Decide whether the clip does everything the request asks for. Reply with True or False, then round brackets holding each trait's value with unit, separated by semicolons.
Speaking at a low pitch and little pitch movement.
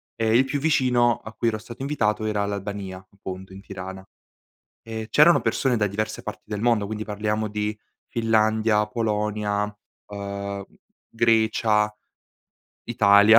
True (105 Hz; 1.8 semitones)